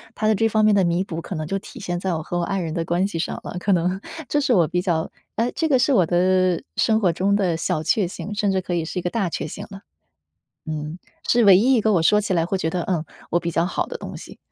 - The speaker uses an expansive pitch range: No, average, 3.5 semitones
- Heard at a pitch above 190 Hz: No, medium, 185 Hz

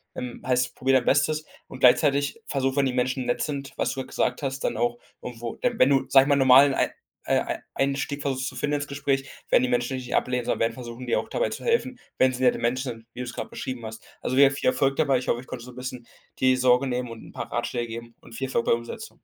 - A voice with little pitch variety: Yes, narrow, 1.9 semitones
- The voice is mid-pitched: No, low, 130 Hz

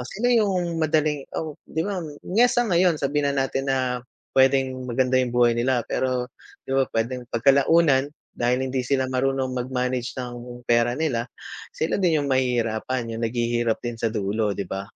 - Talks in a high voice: No, low, 130 Hz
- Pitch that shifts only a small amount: No, average, 3.1 semitones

